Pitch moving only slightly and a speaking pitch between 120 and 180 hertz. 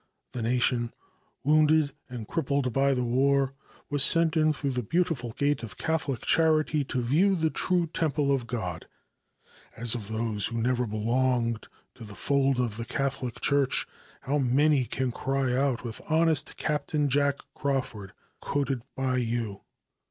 No: average, 3.6 semitones; low, 135 Hz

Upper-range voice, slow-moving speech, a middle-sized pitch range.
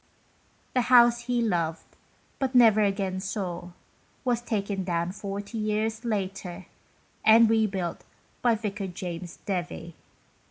Yes: high, 200 Hz; slow, 120 wpm; average, 3.6 semitones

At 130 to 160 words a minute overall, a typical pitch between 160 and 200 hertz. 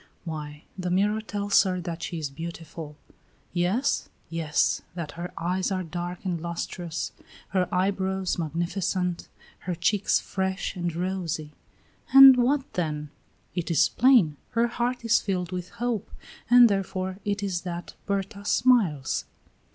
Yes: slow, 135 wpm; medium, 185 Hz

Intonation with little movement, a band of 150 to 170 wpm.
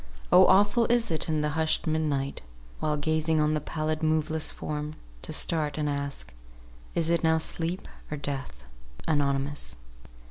Yes: narrow, 1.8 semitones; average, 155 wpm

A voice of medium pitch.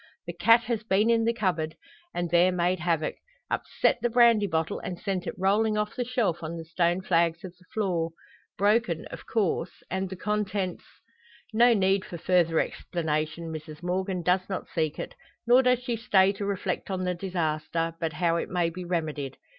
Yes: medium, 180 Hz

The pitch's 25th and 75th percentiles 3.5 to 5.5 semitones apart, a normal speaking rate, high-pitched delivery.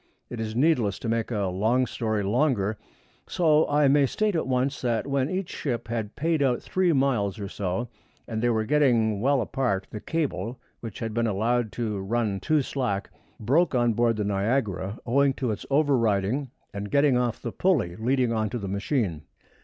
No: average, 4.6 semitones; average, 185 wpm; low, 120 Hz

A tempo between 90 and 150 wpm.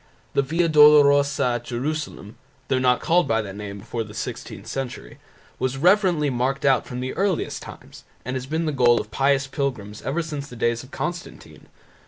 No: average, 185 wpm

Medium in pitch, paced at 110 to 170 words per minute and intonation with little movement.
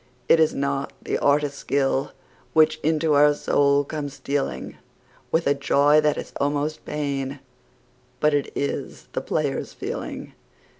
Yes: medium, 145 Hz; average, 140 wpm; narrow, 1.3 semitones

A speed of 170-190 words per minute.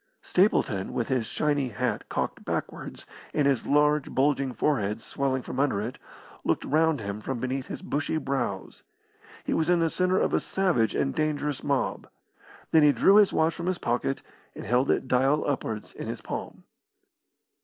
Yes: average, 175 wpm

